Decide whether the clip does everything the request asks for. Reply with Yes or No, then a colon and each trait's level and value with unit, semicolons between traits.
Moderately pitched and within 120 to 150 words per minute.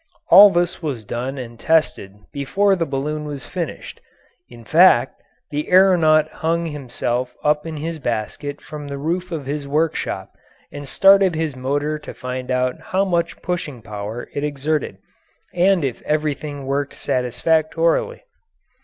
Yes: medium, 150 Hz; average, 145 wpm